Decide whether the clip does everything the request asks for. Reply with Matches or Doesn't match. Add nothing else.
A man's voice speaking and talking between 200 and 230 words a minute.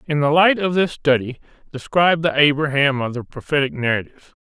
Doesn't match